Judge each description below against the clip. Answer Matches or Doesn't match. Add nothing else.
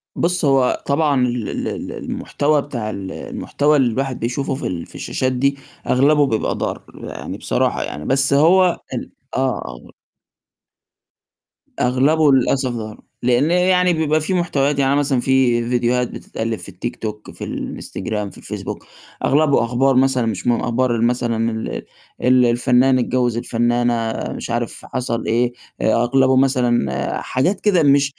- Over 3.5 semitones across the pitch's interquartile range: Doesn't match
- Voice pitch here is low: Matches